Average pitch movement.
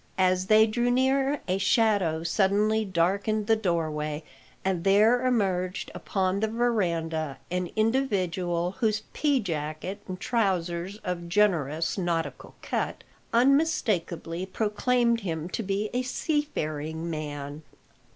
Yes: average, 4.7 semitones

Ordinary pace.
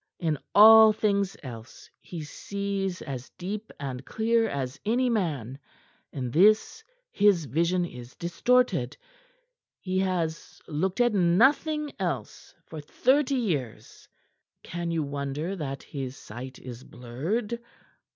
No: slow, 120 wpm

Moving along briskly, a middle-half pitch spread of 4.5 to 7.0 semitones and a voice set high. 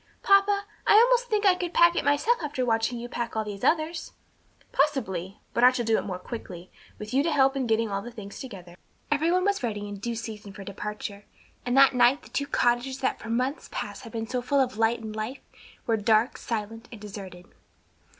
Yes: fast, 220 wpm; average, 4.9 semitones; high, 240 Hz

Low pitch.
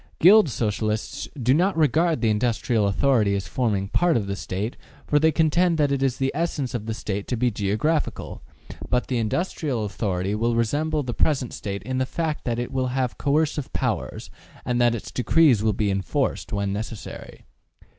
Yes: low, 125 Hz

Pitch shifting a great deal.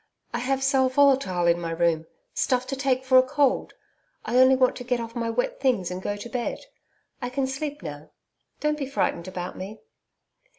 Yes: wide, 6.1 semitones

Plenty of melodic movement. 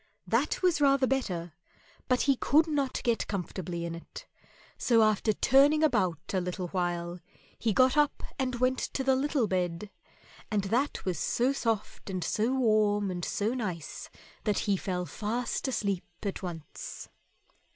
Yes: wide, 6.2 semitones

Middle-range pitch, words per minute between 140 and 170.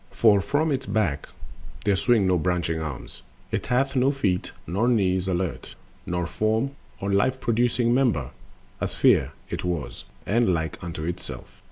No: low, 100 Hz; average, 165 wpm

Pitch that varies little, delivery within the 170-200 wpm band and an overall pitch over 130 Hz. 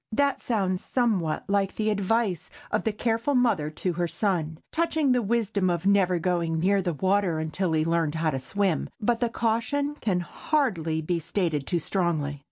No: wide, 5.4 semitones; average, 175 wpm; high, 190 Hz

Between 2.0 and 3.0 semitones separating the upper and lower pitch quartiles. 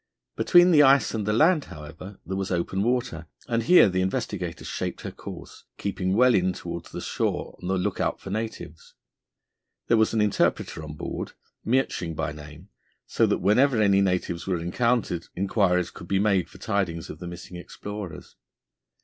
No: average, 4.3 semitones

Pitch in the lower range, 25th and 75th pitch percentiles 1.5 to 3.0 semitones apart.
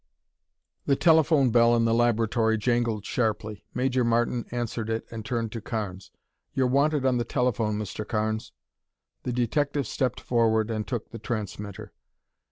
Yes: low, 115 Hz; narrow, 2.4 semitones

